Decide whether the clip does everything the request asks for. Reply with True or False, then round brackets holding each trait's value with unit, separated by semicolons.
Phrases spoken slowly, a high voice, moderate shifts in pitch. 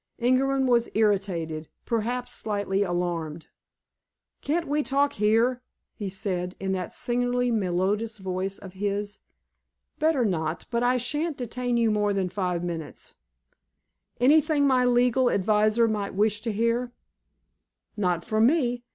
True (125 wpm; 215 Hz; 4.5 semitones)